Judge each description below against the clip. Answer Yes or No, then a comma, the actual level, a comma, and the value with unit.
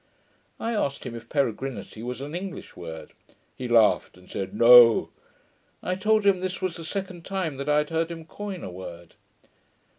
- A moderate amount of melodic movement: No, wide, 7.9 semitones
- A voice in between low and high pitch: Yes, medium, 150 Hz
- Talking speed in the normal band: Yes, average, 180 wpm